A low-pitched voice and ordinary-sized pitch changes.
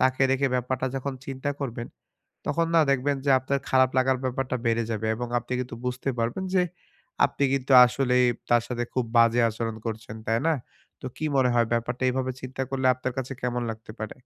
No: low, 125 Hz; narrow, 2.1 semitones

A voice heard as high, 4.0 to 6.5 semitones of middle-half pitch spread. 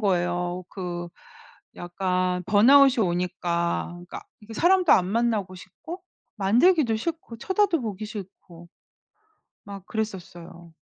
Yes: high, 195 Hz; average, 4.9 semitones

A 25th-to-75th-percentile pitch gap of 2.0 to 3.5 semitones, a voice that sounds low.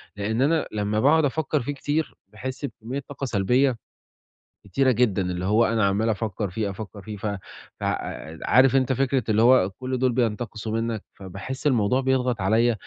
No: average, 3.9 semitones; low, 115 Hz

